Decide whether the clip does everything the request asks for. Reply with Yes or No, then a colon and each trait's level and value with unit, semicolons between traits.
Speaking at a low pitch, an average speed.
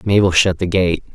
No: very low, 90 Hz; fast, 210 wpm